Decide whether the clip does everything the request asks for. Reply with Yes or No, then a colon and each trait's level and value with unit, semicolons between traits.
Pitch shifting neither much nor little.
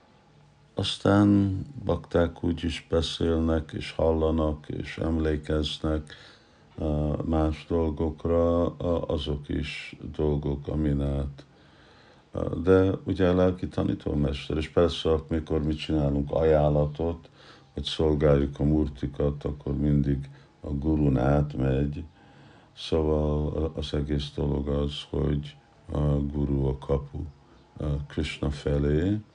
No: narrow, 2.2 semitones